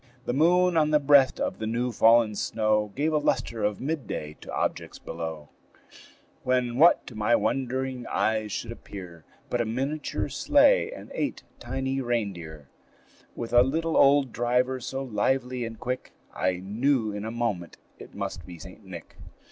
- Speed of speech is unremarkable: Yes, average, 165 wpm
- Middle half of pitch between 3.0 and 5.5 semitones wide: Yes, average, 4.3 semitones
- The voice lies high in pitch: No, low, 120 Hz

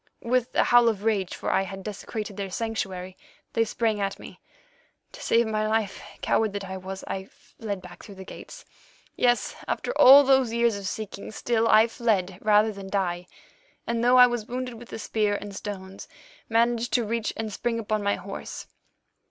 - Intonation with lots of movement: No, average, 3.0 semitones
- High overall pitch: Yes, high, 215 Hz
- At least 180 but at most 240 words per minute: Yes, average, 185 wpm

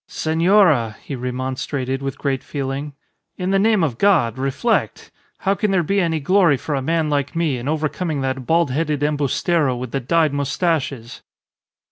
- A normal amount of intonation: Yes, average, 4.0 semitones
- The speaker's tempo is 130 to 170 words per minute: Yes, average, 165 wpm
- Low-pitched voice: No, medium, 145 Hz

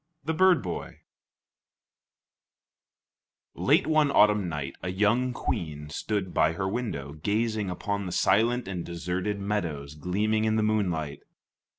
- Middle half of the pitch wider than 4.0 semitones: Yes, average, 4.4 semitones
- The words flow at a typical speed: No, slow, 125 wpm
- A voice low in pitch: Yes, low, 100 Hz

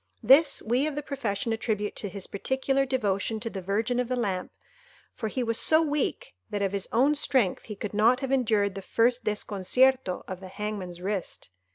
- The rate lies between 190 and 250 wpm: Yes, average, 195 wpm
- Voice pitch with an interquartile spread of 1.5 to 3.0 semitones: No, average, 4.5 semitones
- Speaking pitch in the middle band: No, high, 220 Hz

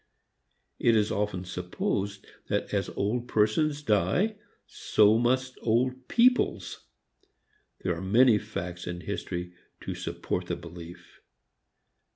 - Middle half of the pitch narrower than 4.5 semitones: No, wide, 5.5 semitones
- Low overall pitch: Yes, low, 105 Hz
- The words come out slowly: Yes, slow, 115 wpm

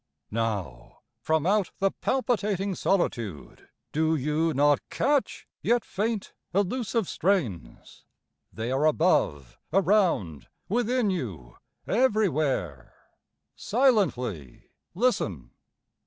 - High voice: No, medium, 165 Hz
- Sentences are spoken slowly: Yes, slow, 85 wpm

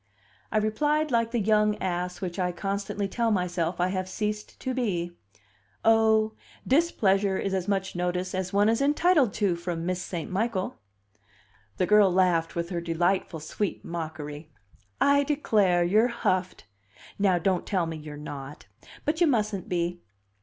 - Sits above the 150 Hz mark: Yes, high, 190 Hz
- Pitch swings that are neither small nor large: Yes, average, 3.7 semitones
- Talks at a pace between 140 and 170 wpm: Yes, average, 155 wpm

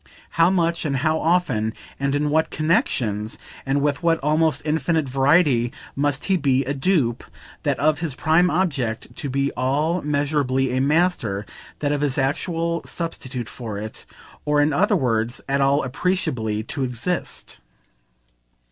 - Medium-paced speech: Yes, average, 155 wpm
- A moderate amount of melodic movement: Yes, average, 3.9 semitones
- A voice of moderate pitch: Yes, medium, 145 Hz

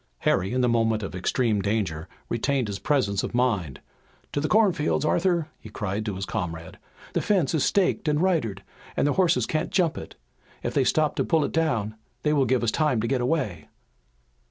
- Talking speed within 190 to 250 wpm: Yes, average, 200 wpm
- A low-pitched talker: Yes, low, 125 Hz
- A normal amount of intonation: No, wide, 7.0 semitones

